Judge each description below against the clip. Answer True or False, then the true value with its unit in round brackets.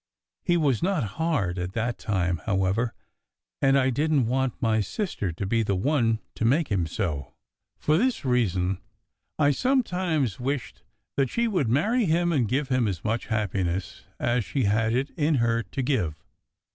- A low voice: True (120 Hz)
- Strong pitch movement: True (6.6 semitones)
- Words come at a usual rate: True (170 wpm)